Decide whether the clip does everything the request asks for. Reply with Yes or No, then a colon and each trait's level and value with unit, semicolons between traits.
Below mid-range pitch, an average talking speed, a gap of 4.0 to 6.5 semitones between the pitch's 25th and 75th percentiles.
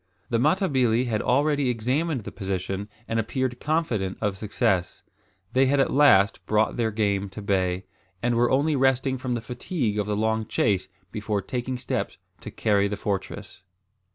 Yes: low, 115 Hz; average, 165 wpm; average, 4.4 semitones